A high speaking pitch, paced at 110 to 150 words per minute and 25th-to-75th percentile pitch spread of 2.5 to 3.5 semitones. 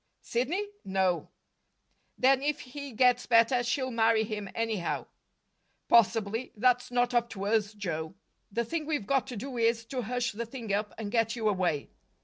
No: high, 230 Hz; average, 165 wpm; average, 3.2 semitones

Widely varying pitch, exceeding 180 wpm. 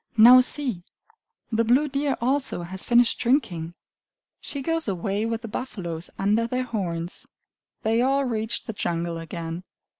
No: wide, 6.4 semitones; average, 145 wpm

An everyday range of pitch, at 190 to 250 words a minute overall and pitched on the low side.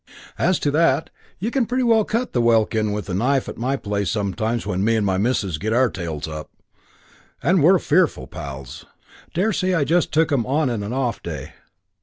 No: wide, 8.2 semitones; average, 195 wpm; low, 120 Hz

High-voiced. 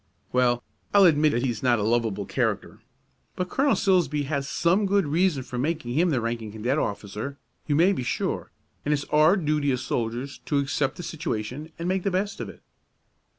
No: medium, 145 Hz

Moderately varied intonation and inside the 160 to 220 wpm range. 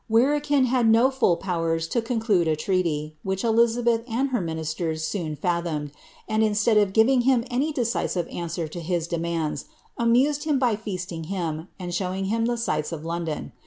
No: wide, 6.0 semitones; average, 170 wpm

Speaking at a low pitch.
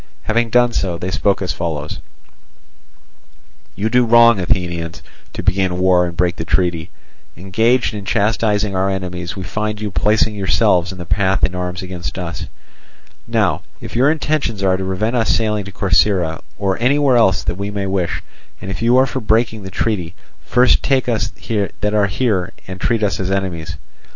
Yes: very low, 95 Hz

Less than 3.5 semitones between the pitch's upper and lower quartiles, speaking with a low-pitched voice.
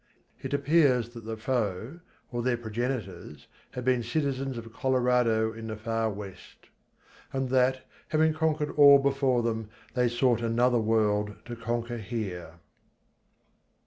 Yes: average, 2.9 semitones; low, 120 Hz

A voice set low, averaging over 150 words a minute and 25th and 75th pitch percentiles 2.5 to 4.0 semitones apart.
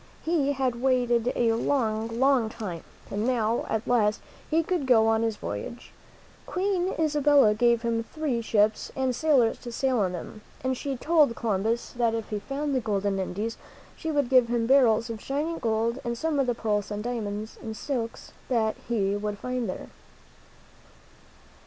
No: high, 235 Hz; average, 170 wpm; average, 3.5 semitones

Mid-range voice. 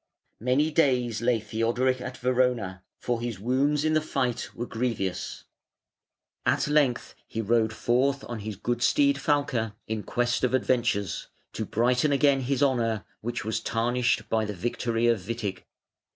No: low, 120 Hz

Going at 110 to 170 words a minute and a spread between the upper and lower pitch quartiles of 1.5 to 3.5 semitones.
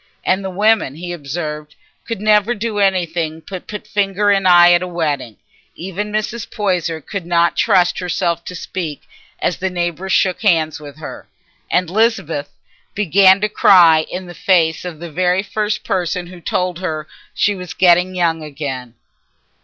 Yes: average, 165 wpm; average, 3.1 semitones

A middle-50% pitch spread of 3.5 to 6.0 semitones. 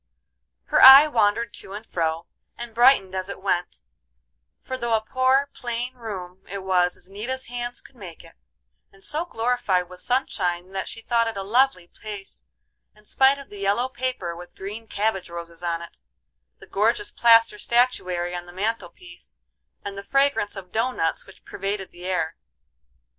Yes: average, 4.9 semitones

